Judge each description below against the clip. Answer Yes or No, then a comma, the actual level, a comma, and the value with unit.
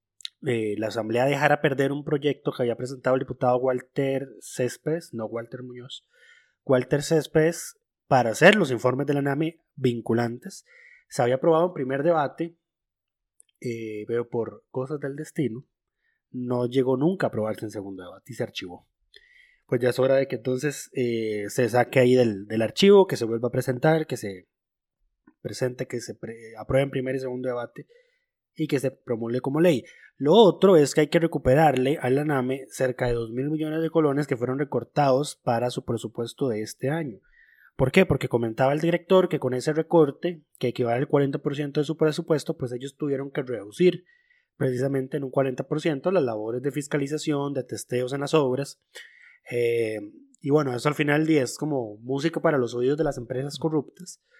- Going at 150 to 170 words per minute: No, average, 185 wpm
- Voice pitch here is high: No, low, 135 Hz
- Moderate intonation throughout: Yes, average, 4.0 semitones